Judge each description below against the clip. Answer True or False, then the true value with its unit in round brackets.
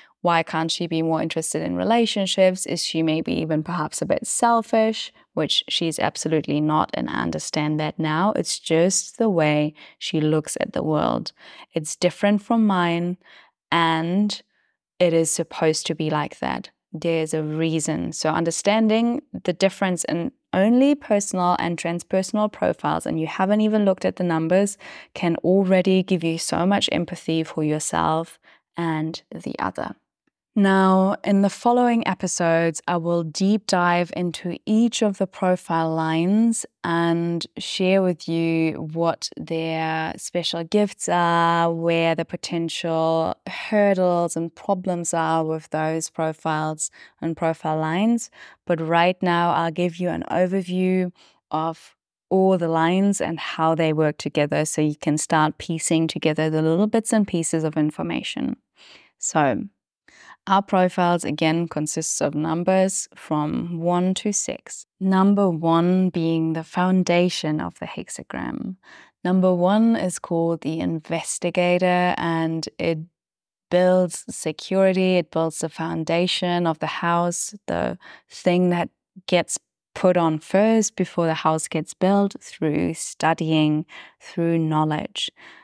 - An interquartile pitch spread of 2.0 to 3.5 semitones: True (2.7 semitones)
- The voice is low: False (170 Hz)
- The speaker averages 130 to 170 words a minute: True (140 wpm)